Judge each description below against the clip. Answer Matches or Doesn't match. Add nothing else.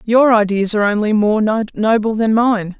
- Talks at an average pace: Matches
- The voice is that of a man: Doesn't match